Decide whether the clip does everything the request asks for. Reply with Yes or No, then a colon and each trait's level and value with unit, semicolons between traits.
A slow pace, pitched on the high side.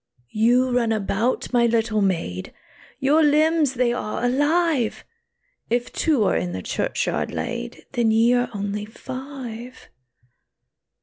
Yes: slow, 125 wpm; high, 240 Hz